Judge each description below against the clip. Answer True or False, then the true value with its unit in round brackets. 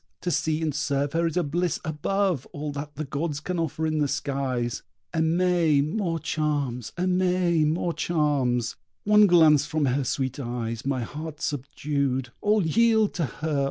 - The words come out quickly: False (155 wpm)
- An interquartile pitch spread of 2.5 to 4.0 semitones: True (3.6 semitones)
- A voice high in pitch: False (150 Hz)